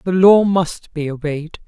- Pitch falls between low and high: Yes, medium, 170 Hz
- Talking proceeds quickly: No, average, 180 wpm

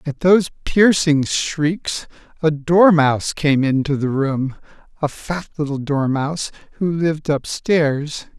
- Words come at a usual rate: No, slow, 120 wpm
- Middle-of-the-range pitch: Yes, medium, 155 Hz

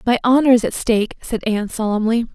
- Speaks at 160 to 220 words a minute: Yes, fast, 205 wpm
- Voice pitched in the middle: No, high, 230 Hz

